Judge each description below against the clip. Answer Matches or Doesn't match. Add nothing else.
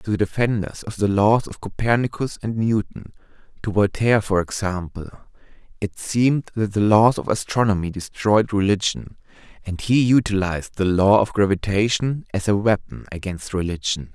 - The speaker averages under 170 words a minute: Matches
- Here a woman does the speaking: Doesn't match